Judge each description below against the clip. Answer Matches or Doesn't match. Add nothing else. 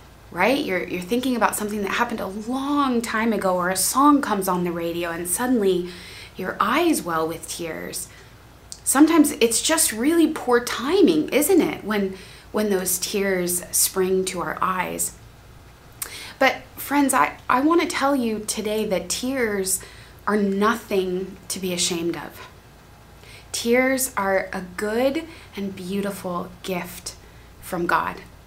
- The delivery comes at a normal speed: Matches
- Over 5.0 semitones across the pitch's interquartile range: Matches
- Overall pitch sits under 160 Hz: Doesn't match